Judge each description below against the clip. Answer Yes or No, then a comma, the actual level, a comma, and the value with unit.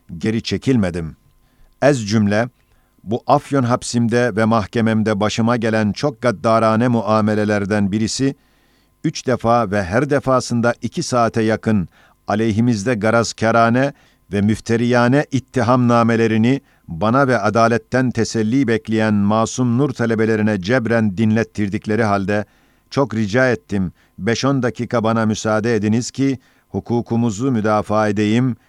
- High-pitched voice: No, low, 115 Hz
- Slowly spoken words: No, average, 110 wpm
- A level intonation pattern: Yes, narrow, 2.3 semitones